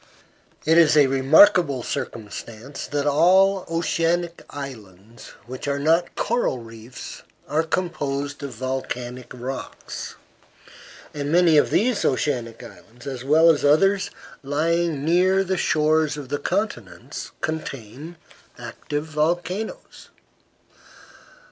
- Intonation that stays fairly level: No, average, 4.3 semitones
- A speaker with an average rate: No, slow, 110 wpm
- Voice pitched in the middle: Yes, medium, 150 Hz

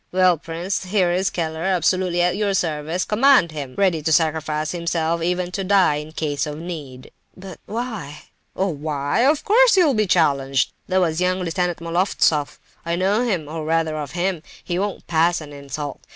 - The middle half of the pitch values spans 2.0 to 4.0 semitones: Yes, average, 3.3 semitones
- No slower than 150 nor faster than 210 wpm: Yes, average, 160 wpm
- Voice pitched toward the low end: No, medium, 170 Hz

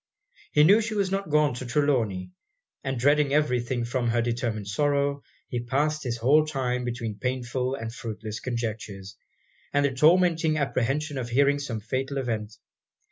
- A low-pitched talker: Yes, low, 130 Hz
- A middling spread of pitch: Yes, average, 3.8 semitones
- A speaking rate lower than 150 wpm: No, average, 165 wpm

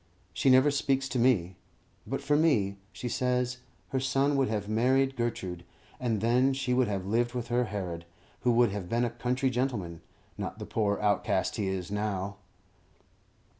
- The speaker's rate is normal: Yes, average, 170 wpm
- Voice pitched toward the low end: Yes, low, 120 Hz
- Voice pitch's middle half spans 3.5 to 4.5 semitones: Yes, average, 4.2 semitones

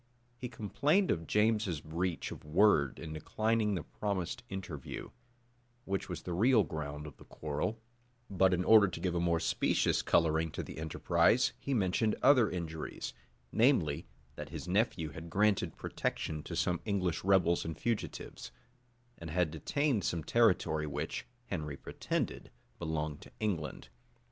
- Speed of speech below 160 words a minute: Yes, average, 150 wpm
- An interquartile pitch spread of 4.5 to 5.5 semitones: Yes, average, 5.1 semitones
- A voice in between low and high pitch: No, very low, 90 Hz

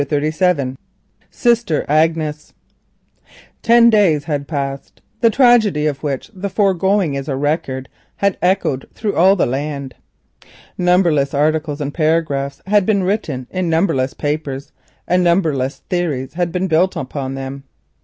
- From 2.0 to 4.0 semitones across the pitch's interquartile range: No, average, 5.0 semitones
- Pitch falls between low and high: Yes, medium, 155 Hz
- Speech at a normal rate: No, slow, 115 wpm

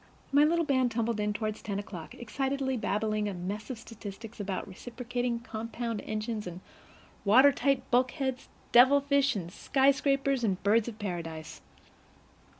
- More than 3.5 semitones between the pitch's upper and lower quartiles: Yes, average, 4.3 semitones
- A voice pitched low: No, high, 230 Hz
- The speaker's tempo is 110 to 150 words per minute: Yes, average, 145 wpm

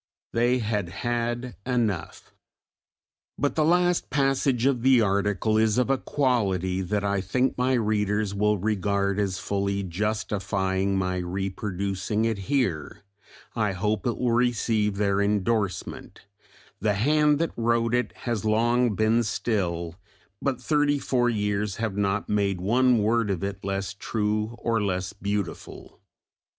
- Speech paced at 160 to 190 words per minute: No, average, 140 wpm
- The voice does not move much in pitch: No, average, 3.4 semitones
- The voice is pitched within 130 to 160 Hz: No, low, 105 Hz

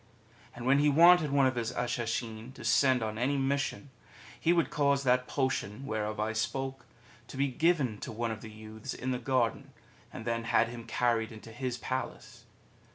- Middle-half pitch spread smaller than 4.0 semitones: Yes, average, 3.4 semitones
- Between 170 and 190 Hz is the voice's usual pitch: No, low, 125 Hz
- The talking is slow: No, average, 190 wpm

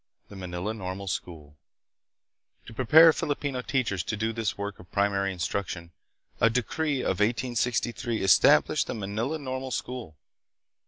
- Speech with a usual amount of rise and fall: Yes, average, 4.6 semitones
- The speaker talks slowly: Yes, slow, 130 wpm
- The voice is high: No, low, 110 Hz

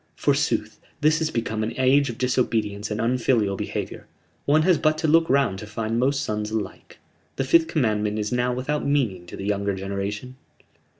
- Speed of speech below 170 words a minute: No, average, 180 wpm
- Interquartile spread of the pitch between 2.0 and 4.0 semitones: No, average, 5.1 semitones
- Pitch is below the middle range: Yes, low, 120 Hz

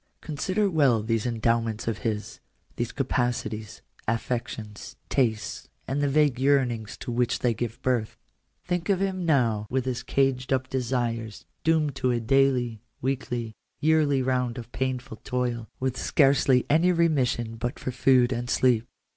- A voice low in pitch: Yes, low, 125 Hz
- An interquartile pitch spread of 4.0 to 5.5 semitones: No, average, 2.9 semitones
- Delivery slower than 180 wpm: Yes, average, 150 wpm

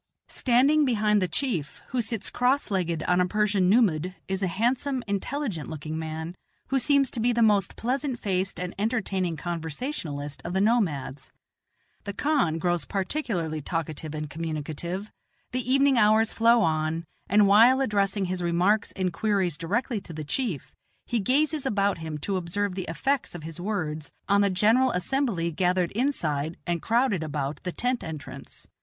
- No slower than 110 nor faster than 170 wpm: Yes, average, 160 wpm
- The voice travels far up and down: Yes, wide, 6.2 semitones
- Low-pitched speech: No, high, 195 Hz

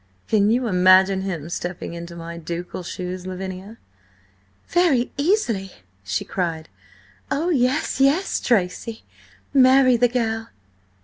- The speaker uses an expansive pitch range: Yes, wide, 6.0 semitones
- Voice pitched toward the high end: Yes, high, 200 Hz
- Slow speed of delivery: Yes, slow, 115 wpm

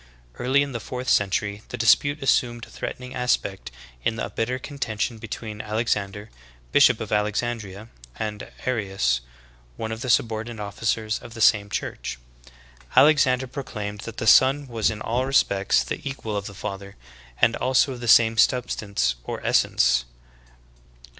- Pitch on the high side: No, low, 110 Hz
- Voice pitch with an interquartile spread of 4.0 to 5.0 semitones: No, average, 3.3 semitones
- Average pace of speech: Yes, average, 155 wpm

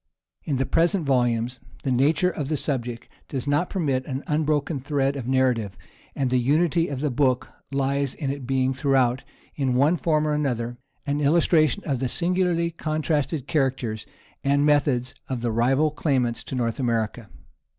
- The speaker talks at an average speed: Yes, average, 165 wpm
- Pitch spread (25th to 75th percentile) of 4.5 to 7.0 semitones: No, average, 3.2 semitones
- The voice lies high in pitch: No, low, 135 Hz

